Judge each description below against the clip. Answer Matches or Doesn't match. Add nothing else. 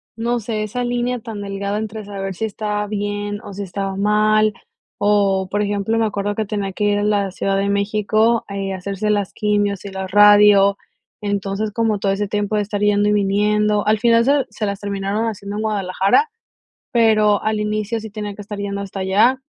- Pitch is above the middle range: Matches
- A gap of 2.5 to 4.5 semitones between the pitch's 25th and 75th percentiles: Doesn't match